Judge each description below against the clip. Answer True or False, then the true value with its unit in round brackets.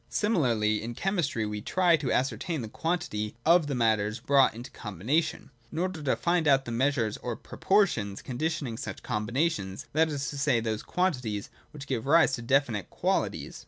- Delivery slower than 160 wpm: False (175 wpm)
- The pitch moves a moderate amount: False (6.3 semitones)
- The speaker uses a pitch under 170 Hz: True (135 Hz)